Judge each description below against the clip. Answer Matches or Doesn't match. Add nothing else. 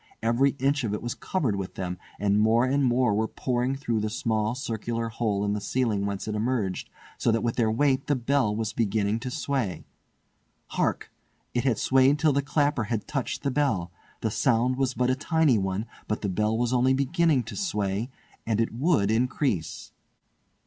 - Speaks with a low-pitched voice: Matches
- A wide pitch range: Doesn't match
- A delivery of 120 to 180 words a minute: Doesn't match